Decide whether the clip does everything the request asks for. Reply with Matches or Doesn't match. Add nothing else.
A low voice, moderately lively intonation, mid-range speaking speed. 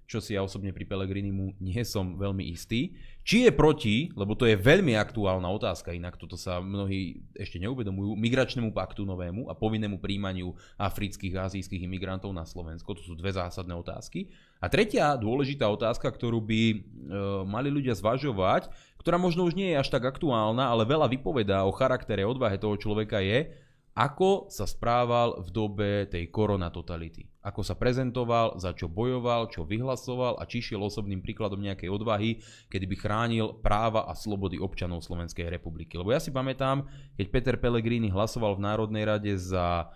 Doesn't match